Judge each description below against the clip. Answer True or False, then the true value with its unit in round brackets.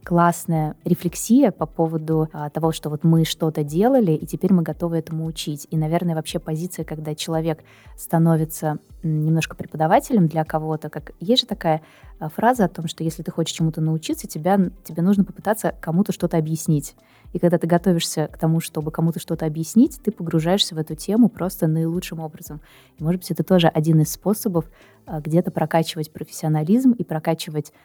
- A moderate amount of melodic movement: False (2.1 semitones)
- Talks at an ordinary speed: False (170 wpm)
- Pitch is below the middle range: False (165 Hz)